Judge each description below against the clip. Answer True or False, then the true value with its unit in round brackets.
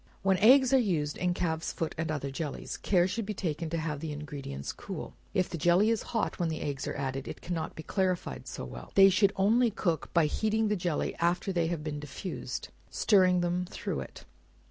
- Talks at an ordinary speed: False (215 wpm)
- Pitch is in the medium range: True (175 Hz)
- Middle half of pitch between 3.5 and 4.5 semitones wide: True (4.1 semitones)